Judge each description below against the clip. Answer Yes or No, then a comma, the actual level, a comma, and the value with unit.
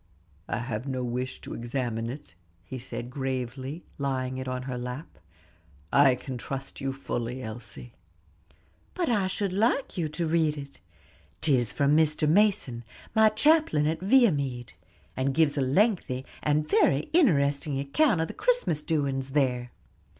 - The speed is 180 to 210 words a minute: No, average, 150 wpm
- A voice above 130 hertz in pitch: Yes, medium, 140 Hz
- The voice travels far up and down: No, average, 4.1 semitones